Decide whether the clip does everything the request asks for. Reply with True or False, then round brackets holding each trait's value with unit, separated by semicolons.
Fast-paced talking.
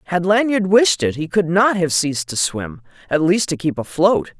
True (220 wpm)